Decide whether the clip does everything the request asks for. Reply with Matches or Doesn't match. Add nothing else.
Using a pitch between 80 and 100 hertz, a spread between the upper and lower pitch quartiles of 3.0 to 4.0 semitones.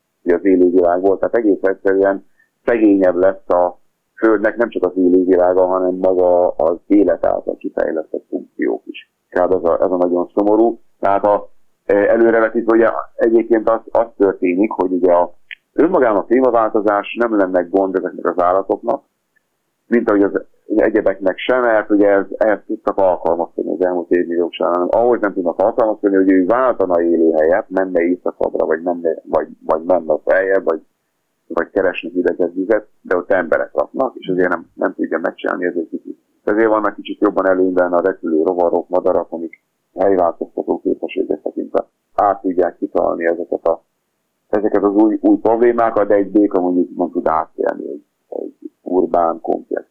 Matches